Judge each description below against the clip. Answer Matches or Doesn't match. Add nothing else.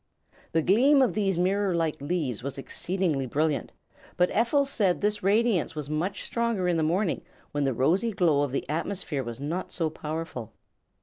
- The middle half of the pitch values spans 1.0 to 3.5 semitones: Doesn't match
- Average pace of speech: Matches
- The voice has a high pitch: Doesn't match